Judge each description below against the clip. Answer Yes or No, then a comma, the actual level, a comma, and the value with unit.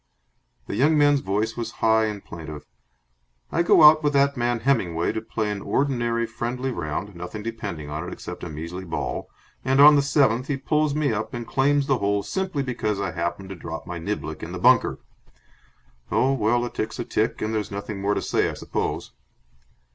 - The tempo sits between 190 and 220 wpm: Yes, average, 200 wpm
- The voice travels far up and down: Yes, wide, 5.7 semitones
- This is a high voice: No, low, 115 Hz